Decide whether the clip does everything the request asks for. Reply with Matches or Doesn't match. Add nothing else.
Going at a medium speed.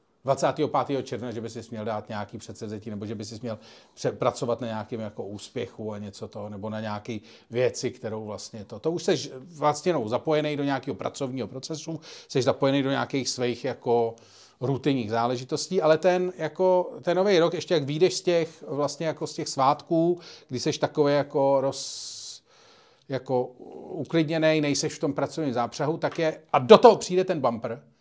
Doesn't match